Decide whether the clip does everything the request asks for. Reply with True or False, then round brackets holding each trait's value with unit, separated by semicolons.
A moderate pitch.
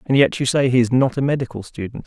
False (130 Hz)